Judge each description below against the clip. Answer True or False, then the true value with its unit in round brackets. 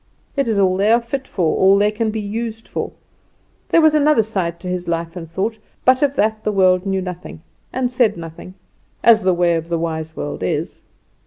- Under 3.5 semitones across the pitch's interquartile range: False (4.8 semitones)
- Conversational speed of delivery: False (215 wpm)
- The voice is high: True (195 Hz)